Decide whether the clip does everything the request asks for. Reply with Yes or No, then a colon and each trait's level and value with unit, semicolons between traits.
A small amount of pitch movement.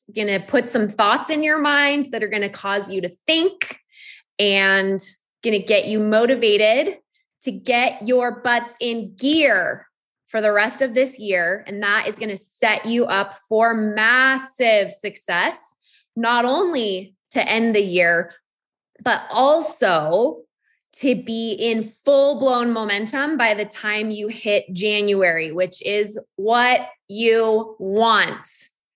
No: average, 4.0 semitones